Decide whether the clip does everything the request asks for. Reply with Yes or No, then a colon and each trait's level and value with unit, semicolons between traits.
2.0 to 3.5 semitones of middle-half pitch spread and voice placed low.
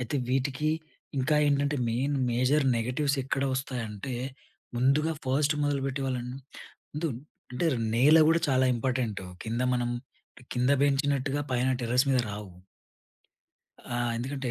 Yes: narrow, 2.6 semitones; low, 130 Hz